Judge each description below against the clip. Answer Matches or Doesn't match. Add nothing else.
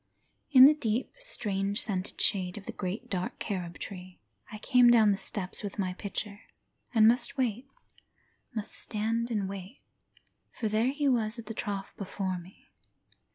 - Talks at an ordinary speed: Matches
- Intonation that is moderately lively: Matches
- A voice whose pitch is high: Matches